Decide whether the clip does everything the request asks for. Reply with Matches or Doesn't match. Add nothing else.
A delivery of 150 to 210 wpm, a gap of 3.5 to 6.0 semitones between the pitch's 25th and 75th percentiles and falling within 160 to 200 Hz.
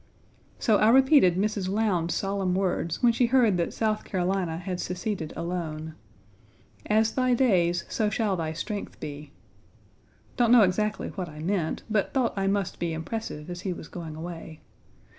Matches